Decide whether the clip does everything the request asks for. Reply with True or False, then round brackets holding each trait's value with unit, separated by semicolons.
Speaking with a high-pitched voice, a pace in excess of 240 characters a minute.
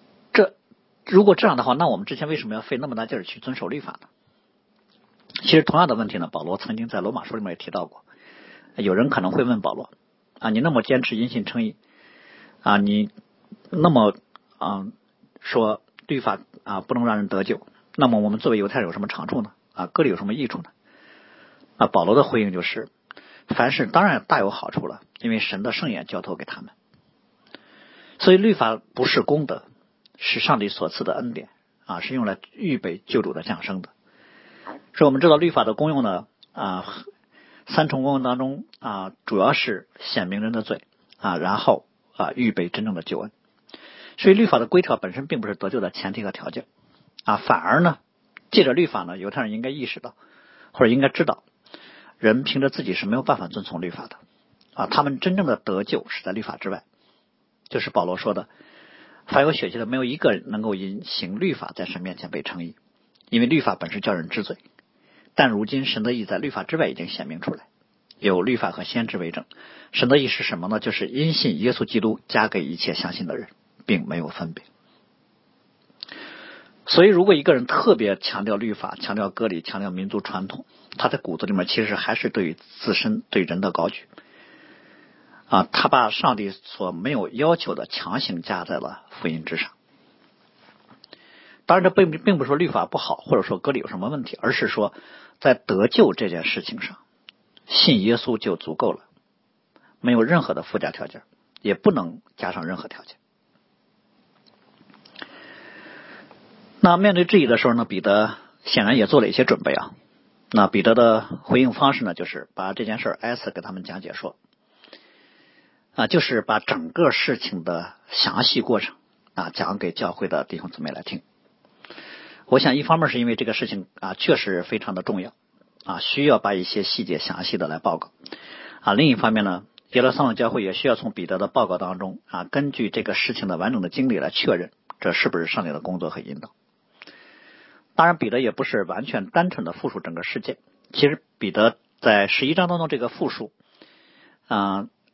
False (150 Hz; 280 characters per minute)